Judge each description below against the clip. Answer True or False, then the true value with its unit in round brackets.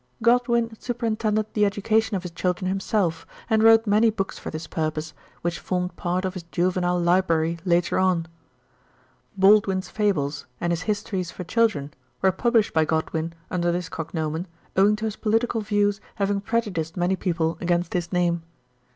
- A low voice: False (185 Hz)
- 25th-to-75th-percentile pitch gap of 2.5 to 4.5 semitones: True (3.7 semitones)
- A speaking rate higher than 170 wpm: False (160 wpm)